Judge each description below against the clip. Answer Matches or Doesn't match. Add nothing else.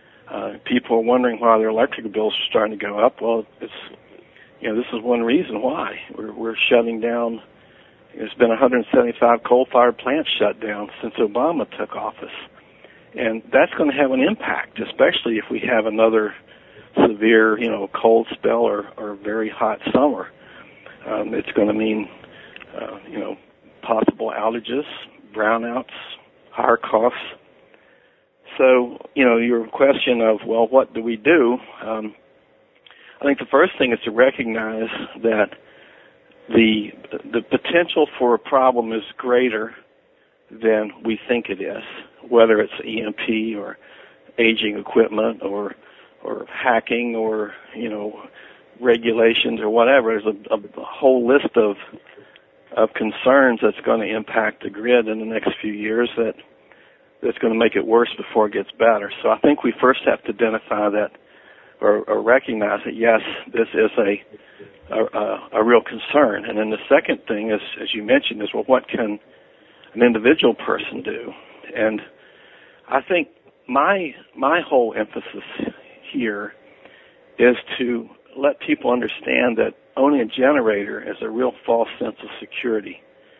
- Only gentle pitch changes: Matches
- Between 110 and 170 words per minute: Matches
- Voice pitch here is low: Matches